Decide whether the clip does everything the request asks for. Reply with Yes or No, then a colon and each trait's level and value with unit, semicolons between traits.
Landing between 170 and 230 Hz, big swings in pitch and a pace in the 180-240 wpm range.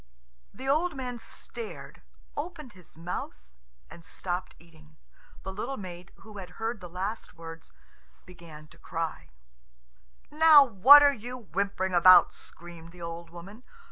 No: medium, 185 Hz; wide, 6.4 semitones; average, 140 wpm